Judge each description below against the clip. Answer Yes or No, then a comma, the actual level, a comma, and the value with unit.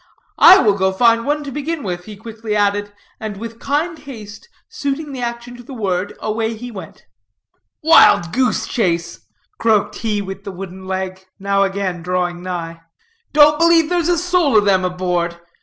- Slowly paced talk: No, average, 175 wpm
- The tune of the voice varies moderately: No, wide, 6.3 semitones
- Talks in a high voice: Yes, high, 210 Hz